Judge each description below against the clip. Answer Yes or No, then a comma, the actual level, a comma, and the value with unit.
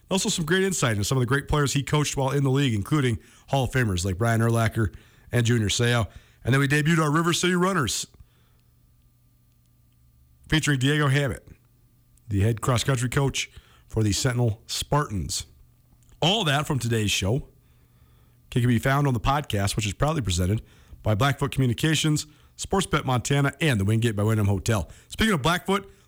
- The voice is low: Yes, low, 125 Hz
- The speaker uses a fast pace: No, average, 170 wpm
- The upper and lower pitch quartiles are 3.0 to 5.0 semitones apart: No, wide, 5.6 semitones